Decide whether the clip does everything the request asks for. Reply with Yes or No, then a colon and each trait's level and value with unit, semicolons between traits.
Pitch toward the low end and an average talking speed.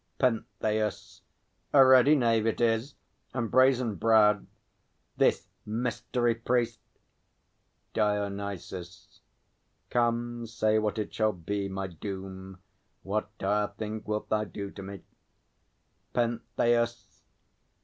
No: low, 110 Hz; slow, 100 wpm